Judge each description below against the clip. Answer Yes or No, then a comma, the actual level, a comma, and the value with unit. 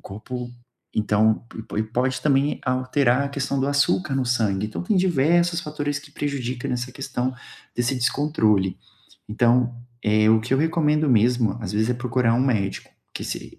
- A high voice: No, low, 125 Hz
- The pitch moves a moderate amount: Yes, average, 4.0 semitones